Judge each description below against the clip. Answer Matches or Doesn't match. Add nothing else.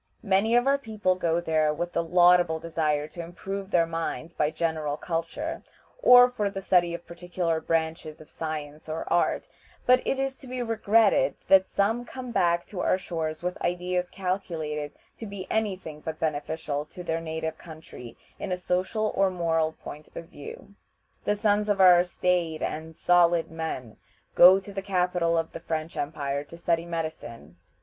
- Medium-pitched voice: Matches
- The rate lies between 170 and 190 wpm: Matches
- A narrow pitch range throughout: Doesn't match